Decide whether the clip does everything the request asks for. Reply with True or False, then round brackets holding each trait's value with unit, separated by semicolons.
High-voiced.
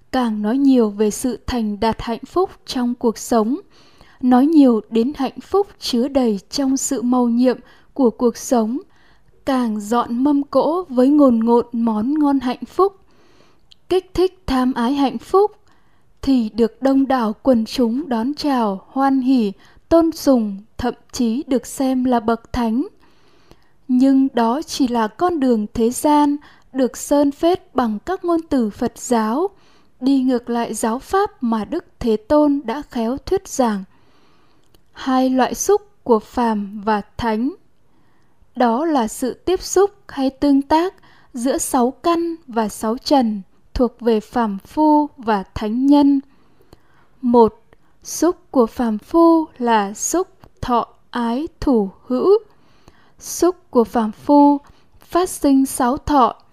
True (255 Hz)